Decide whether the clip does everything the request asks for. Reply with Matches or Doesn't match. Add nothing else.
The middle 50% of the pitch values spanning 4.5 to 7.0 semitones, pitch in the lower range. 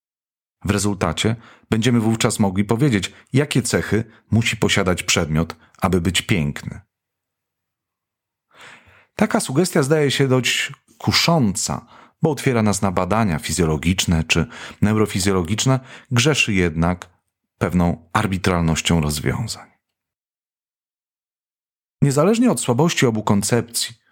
Matches